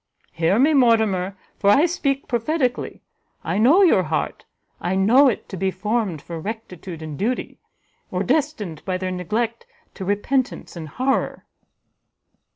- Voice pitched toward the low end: No, high, 210 Hz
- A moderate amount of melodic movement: No, wide, 5.7 semitones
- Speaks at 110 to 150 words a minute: Yes, average, 145 wpm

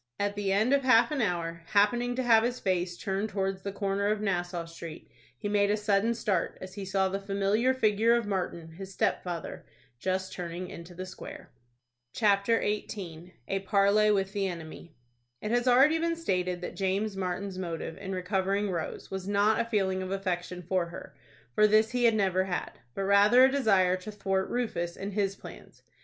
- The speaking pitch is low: No, high, 195 Hz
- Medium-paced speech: Yes, average, 190 wpm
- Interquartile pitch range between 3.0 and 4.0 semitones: No, narrow, 2.5 semitones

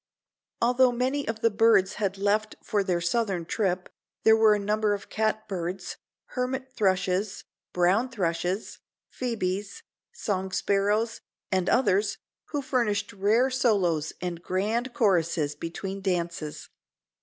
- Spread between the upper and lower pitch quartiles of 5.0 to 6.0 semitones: No, average, 3.6 semitones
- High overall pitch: Yes, high, 205 Hz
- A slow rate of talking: Yes, slow, 120 wpm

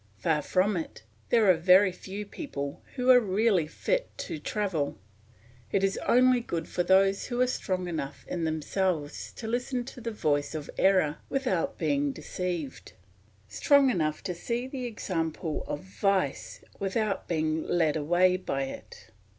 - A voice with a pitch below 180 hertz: No, medium, 185 Hz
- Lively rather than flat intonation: Yes, wide, 6.6 semitones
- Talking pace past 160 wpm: No, average, 155 wpm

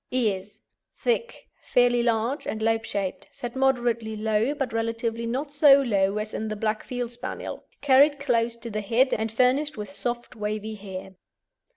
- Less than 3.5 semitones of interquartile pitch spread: Yes, average, 3.0 semitones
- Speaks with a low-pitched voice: No, high, 230 Hz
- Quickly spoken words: No, average, 165 wpm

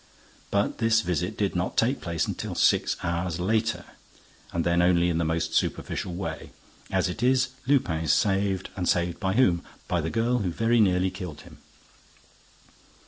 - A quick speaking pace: No, average, 170 wpm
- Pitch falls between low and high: No, very low, 90 Hz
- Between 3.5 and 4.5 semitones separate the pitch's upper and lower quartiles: Yes, average, 4.2 semitones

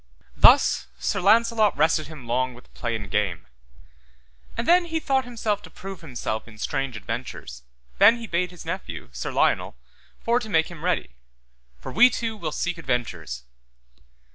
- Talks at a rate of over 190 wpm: No, average, 165 wpm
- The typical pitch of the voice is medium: Yes, medium, 165 Hz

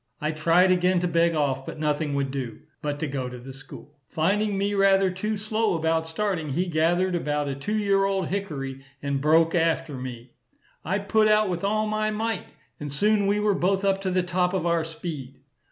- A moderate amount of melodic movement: Yes, average, 5.0 semitones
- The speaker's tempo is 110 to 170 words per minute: No, fast, 205 wpm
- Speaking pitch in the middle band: Yes, medium, 170 Hz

